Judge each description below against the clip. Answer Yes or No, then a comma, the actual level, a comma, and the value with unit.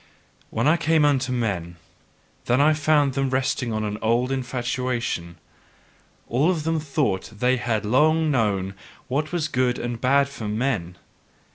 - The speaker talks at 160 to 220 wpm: No, average, 150 wpm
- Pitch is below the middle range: Yes, low, 125 Hz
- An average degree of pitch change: Yes, average, 4.4 semitones